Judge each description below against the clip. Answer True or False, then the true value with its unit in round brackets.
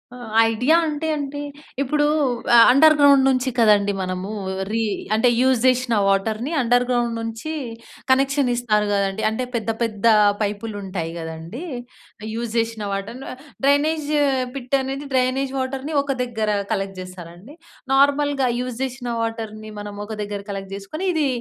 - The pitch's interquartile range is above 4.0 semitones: True (4.5 semitones)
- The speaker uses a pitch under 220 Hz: False (235 Hz)